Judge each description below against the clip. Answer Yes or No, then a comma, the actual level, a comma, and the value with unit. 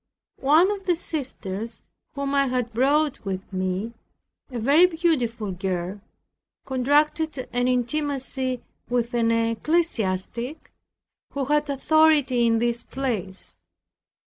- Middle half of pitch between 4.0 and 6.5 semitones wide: Yes, average, 4.4 semitones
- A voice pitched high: Yes, very high, 255 Hz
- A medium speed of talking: No, slow, 110 wpm